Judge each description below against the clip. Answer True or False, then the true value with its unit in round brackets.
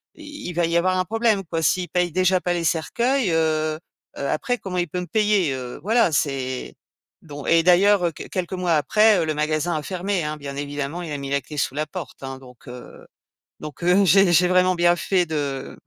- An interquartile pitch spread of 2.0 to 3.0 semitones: False (3.6 semitones)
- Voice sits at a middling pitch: True (170 Hz)